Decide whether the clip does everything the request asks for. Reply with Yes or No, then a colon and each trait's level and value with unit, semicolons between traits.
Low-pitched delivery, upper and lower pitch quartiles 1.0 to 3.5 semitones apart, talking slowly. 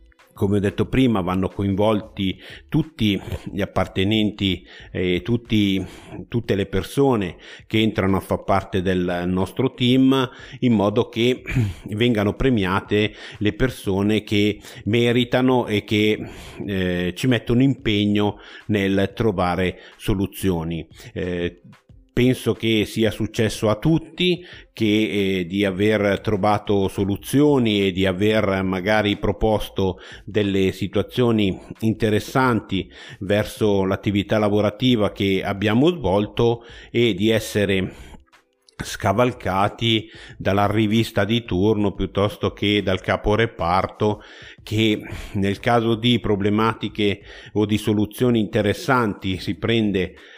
Yes: low, 105 Hz; average, 2.7 semitones; slow, 105 wpm